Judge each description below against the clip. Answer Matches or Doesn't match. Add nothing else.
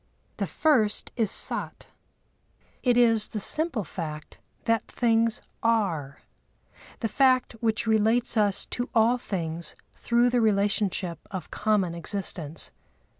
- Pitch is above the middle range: Matches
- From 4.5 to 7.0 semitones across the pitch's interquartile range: Doesn't match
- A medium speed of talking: Doesn't match